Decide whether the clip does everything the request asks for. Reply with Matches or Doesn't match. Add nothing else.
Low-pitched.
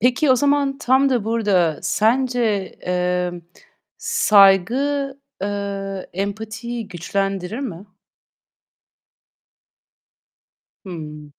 Doesn't match